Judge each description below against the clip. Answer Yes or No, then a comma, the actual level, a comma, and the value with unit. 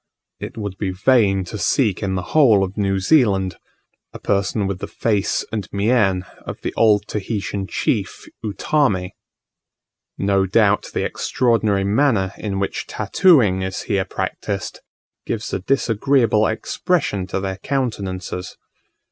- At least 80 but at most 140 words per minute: Yes, slow, 135 wpm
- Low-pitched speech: Yes, low, 100 Hz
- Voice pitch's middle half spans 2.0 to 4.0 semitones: Yes, average, 2.9 semitones